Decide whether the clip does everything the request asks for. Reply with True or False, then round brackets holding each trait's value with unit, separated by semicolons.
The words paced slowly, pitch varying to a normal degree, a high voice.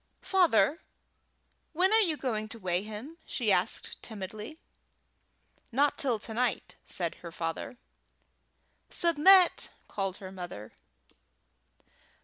False (110 wpm; 8.6 semitones; 225 Hz)